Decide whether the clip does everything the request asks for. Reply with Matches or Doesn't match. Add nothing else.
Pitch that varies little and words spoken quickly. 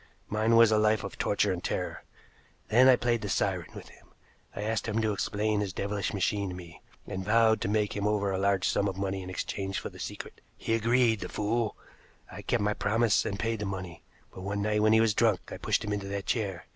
Matches